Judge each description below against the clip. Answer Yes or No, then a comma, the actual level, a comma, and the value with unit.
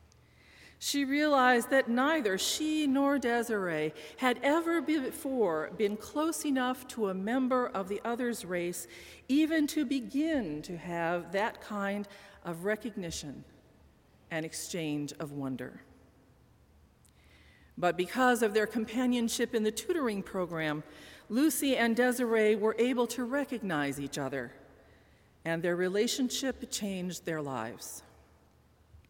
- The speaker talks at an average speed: No, slow, 120 wpm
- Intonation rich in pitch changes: Yes, wide, 7.5 semitones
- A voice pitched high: Yes, high, 215 Hz